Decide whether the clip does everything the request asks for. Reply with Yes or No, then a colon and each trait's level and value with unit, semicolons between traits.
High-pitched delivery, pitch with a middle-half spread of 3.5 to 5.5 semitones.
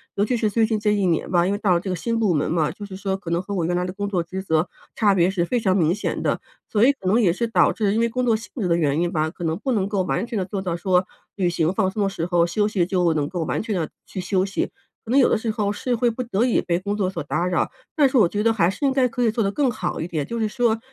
Yes: high, 195 Hz; average, 4.0 semitones